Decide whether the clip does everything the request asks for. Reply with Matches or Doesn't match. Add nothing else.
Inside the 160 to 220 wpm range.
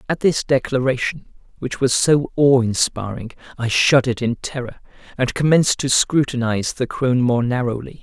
Doesn't match